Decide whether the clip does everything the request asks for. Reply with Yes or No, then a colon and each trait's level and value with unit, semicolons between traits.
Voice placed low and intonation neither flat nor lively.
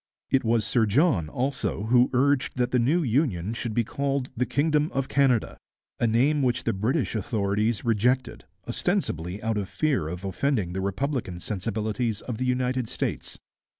Yes: low, 120 Hz; average, 4.2 semitones